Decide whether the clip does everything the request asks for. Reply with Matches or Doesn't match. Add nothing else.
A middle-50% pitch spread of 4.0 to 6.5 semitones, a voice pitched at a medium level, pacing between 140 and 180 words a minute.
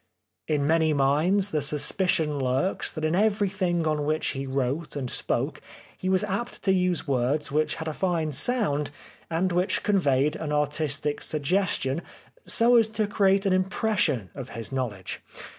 Matches